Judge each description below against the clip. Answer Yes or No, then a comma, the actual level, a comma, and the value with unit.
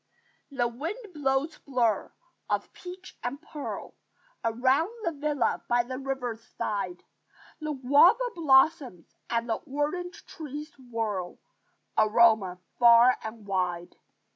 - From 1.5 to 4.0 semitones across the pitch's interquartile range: No, average, 4.8 semitones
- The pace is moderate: No, slow, 115 wpm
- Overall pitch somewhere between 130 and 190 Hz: No, very high, 260 Hz